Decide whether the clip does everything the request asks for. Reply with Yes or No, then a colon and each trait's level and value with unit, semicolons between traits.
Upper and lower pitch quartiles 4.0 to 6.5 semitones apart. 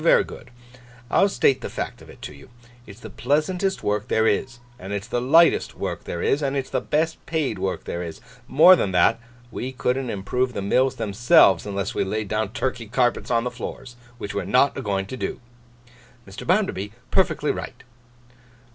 Yes: average, 4.9 semitones